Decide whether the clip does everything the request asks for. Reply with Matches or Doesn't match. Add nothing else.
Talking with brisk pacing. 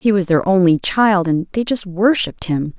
Matches